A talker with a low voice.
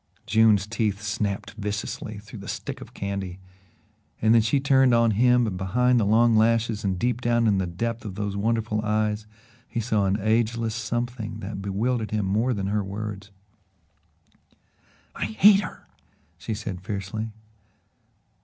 Yes: low, 110 Hz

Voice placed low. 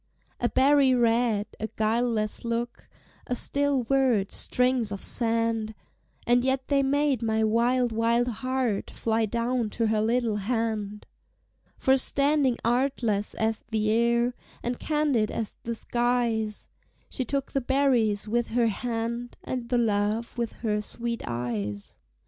No: high, 235 Hz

